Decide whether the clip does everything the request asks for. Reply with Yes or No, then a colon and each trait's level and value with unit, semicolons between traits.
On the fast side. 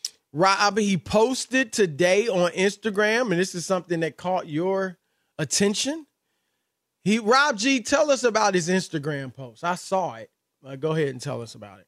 No: average, 170 wpm